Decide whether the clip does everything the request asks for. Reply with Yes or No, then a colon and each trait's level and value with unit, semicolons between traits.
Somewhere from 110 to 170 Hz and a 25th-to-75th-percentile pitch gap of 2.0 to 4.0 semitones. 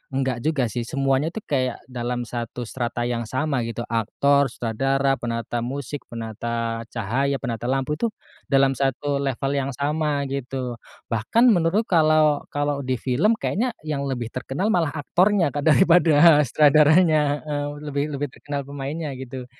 Yes: medium, 140 Hz; average, 3.5 semitones